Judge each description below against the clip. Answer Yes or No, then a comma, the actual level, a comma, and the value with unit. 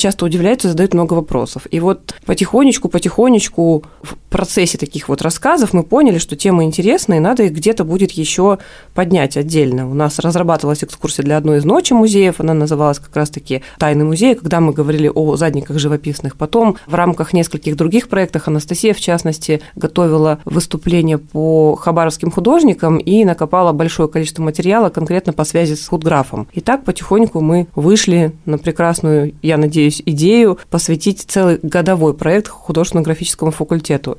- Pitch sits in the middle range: Yes, medium, 165 Hz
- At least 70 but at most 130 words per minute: No, average, 155 wpm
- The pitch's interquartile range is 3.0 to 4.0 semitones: Yes, average, 3.4 semitones